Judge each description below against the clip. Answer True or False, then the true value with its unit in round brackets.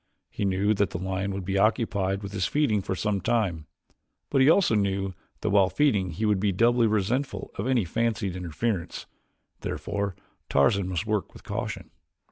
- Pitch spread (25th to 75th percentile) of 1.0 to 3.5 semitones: True (2.9 semitones)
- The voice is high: False (100 Hz)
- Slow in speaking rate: False (175 wpm)